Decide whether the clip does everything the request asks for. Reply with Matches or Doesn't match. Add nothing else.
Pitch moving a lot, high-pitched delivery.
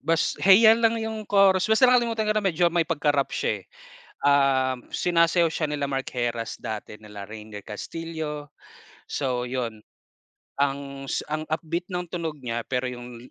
Doesn't match